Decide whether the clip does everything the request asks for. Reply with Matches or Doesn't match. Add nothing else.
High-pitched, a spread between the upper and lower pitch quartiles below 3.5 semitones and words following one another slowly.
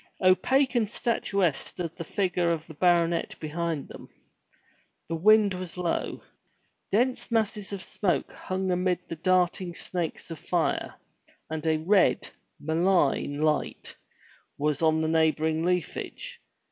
Doesn't match